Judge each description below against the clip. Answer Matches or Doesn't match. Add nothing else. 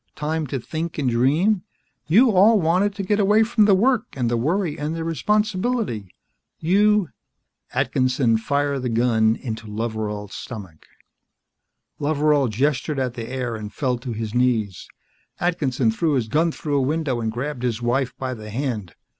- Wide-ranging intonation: Matches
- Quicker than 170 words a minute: Doesn't match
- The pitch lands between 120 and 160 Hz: Matches